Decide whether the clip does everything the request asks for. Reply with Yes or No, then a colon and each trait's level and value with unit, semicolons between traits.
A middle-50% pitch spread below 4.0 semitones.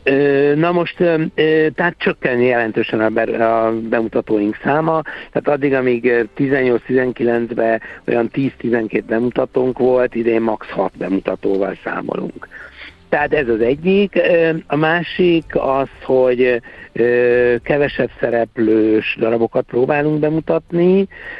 No: average, 5.1 semitones